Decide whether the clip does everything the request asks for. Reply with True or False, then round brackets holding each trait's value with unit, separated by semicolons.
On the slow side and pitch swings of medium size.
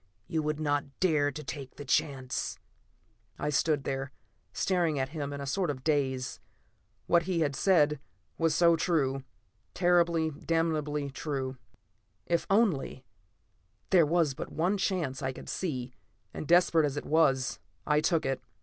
False (150 wpm; 3.5 semitones)